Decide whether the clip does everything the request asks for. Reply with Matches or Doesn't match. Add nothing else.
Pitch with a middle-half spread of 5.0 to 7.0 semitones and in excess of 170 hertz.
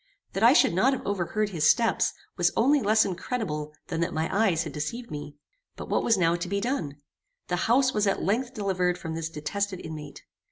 Matches